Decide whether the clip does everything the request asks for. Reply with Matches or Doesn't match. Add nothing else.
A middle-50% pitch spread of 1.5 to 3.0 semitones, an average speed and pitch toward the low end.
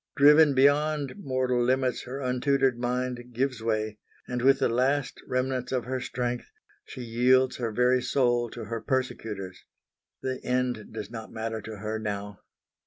Matches